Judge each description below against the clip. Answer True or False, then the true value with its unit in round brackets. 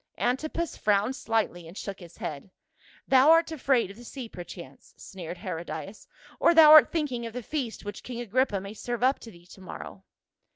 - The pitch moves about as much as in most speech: False (5.7 semitones)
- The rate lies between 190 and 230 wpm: True (195 wpm)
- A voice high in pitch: True (225 Hz)